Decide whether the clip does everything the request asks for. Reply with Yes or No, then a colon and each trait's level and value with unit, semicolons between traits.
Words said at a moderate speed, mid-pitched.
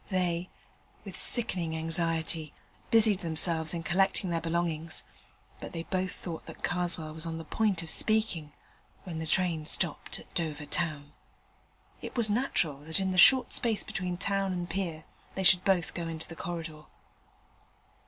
Yes: average, 160 wpm; medium, 170 Hz